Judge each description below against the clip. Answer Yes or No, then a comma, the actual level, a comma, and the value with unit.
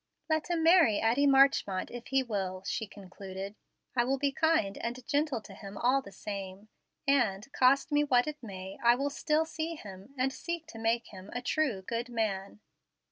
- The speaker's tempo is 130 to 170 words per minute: No, average, 190 wpm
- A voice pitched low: No, high, 240 Hz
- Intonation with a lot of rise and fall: Yes, wide, 6.0 semitones